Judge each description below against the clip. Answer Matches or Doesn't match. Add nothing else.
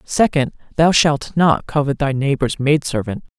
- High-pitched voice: Doesn't match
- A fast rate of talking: Doesn't match